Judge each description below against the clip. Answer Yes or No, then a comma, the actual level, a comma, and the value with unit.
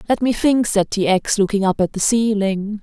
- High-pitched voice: Yes, high, 210 Hz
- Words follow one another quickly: Yes, fast, 235 wpm